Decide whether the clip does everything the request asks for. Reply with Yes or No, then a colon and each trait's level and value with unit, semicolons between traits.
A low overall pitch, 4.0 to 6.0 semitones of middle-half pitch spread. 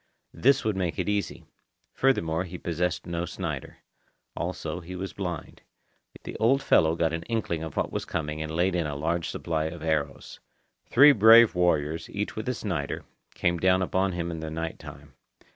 No: very low, 85 Hz; average, 3.3 semitones